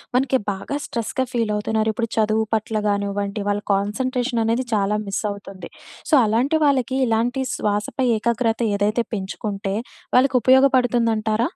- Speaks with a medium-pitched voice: No, high, 225 Hz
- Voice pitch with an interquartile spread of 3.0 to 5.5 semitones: Yes, average, 3.3 semitones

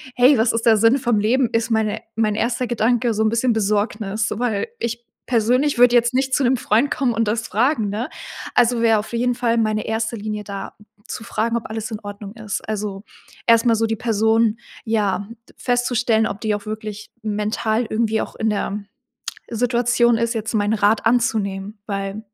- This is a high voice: Yes, high, 225 Hz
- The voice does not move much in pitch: Yes, narrow, 2.0 semitones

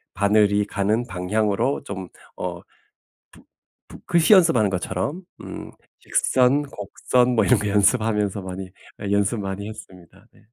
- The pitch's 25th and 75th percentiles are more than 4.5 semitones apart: No, average, 3.8 semitones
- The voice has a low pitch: Yes, low, 105 Hz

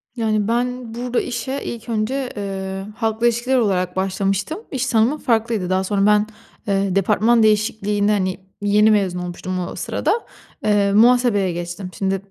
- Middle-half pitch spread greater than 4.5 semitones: No, average, 3.4 semitones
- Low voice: No, high, 210 Hz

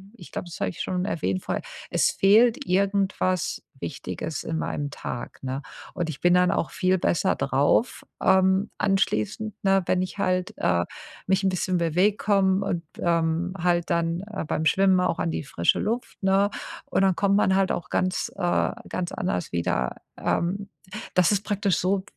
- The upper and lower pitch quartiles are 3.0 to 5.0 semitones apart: No, narrow, 2.6 semitones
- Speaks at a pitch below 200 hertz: Yes, medium, 185 Hz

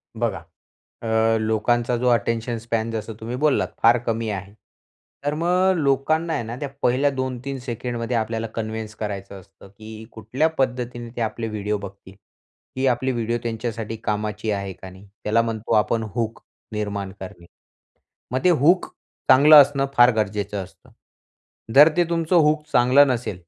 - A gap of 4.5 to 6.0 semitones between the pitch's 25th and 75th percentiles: No, average, 3.3 semitones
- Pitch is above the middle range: No, low, 115 Hz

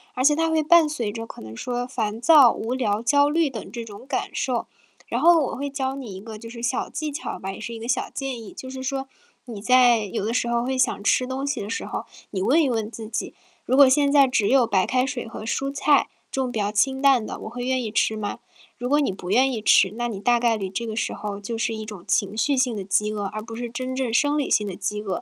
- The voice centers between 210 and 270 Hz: Yes, high, 240 Hz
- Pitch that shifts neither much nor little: Yes, average, 3.8 semitones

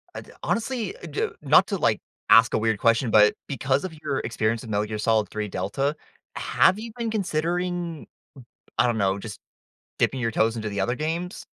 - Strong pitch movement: Yes, wide, 7.8 semitones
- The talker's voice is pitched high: No, low, 125 Hz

